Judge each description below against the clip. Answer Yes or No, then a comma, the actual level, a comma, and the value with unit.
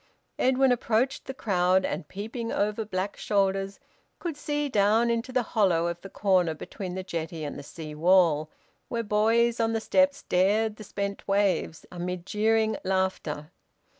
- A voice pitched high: Yes, high, 200 Hz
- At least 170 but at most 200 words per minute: No, average, 160 wpm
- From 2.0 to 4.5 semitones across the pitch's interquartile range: Yes, average, 3.9 semitones